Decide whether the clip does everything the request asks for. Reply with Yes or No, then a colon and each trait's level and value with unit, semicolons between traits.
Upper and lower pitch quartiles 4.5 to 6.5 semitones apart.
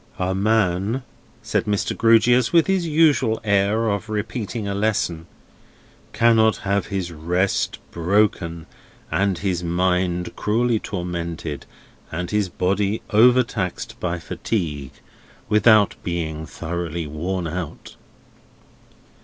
No: average, 4.0 semitones